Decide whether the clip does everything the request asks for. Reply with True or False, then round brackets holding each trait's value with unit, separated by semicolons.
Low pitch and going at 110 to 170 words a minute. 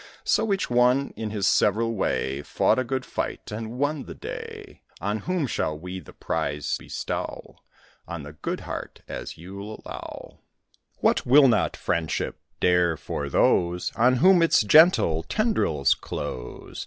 True (110 Hz; 150 wpm)